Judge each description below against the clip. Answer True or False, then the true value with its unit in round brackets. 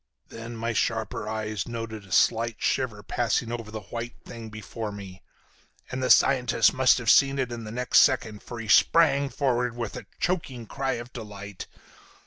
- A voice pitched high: False (115 Hz)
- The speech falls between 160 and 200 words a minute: True (175 wpm)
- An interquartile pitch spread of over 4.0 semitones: False (2.4 semitones)